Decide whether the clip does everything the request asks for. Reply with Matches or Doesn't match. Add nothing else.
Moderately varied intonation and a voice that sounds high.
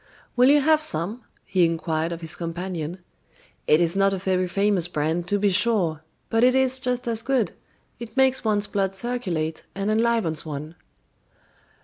Doesn't match